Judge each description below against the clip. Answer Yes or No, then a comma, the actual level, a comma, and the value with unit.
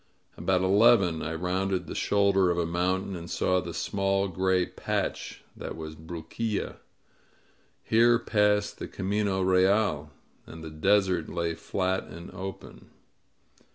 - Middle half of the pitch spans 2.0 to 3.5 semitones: Yes, narrow, 2.6 semitones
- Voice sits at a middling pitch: No, very low, 95 Hz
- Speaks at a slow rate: Yes, slow, 130 wpm